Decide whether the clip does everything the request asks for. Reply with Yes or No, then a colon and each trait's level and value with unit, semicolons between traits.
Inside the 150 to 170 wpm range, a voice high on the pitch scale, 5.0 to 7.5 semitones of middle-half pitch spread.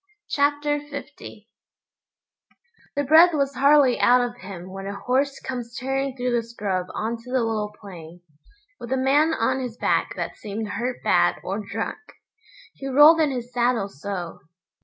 No: average, 160 wpm; very high, 250 Hz; average, 4.5 semitones